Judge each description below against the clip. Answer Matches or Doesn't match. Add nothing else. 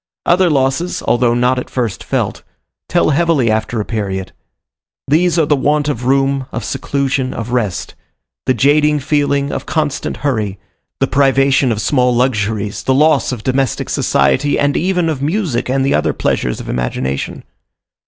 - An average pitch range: Matches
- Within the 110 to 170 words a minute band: Matches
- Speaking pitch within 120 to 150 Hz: Matches